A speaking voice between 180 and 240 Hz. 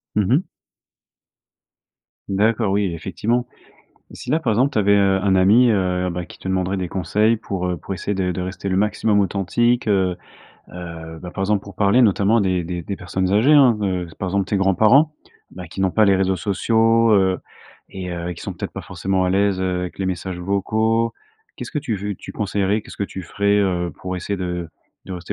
No: very low, 95 Hz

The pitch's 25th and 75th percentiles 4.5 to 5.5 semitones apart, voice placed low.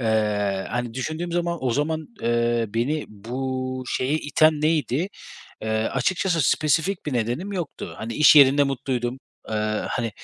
Yes: average, 4.9 semitones; low, 130 Hz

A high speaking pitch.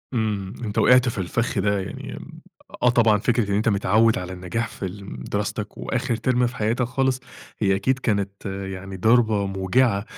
No: low, 105 Hz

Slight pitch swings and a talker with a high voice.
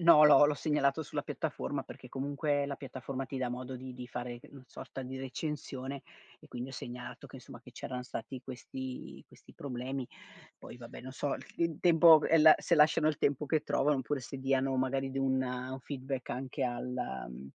No: narrow, 2.1 semitones; low, 135 Hz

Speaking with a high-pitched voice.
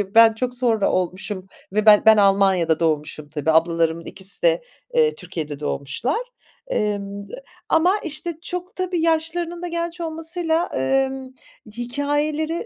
Yes: very high, 250 Hz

